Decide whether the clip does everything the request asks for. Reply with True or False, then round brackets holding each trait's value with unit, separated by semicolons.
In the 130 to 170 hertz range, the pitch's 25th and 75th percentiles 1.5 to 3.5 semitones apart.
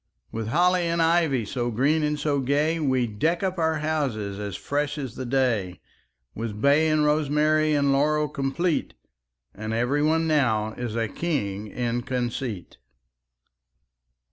False (140 Hz; 4.9 semitones)